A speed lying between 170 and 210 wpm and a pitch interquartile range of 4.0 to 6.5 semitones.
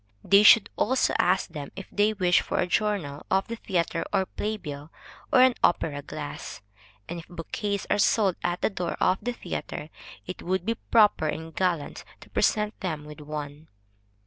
Yes: average, 180 wpm; average, 4.8 semitones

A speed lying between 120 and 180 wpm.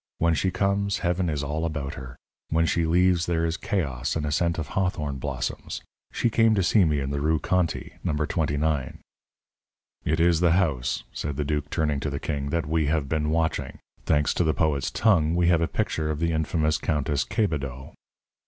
No: average, 200 wpm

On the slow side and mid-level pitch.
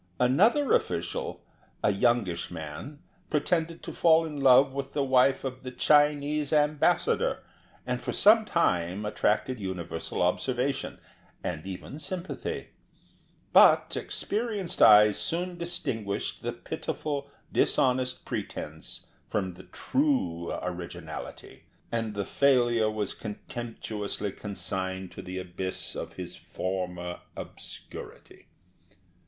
No: slow, 110 wpm; low, 125 Hz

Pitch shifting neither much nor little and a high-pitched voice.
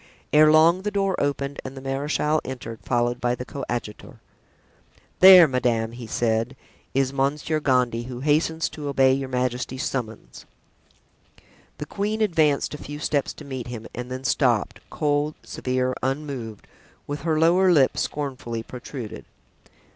No: average, 3.5 semitones; low, 135 Hz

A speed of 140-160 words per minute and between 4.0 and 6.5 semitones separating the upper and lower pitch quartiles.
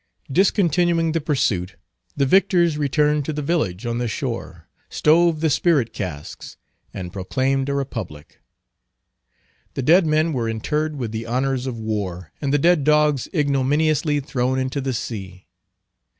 Yes: average, 145 wpm; average, 5.0 semitones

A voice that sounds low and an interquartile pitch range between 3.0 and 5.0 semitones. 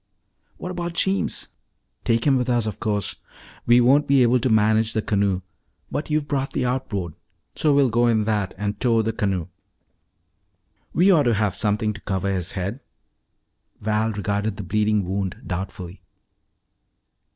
Yes: low, 110 Hz; average, 3.8 semitones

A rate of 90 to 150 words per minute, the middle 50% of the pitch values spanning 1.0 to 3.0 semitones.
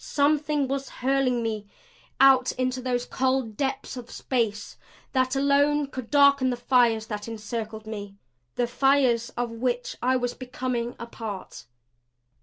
Yes: average, 140 wpm; average, 2.7 semitones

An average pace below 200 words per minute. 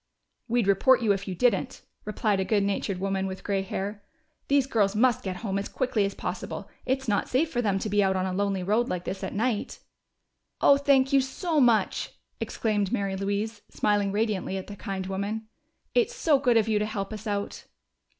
No: fast, 205 wpm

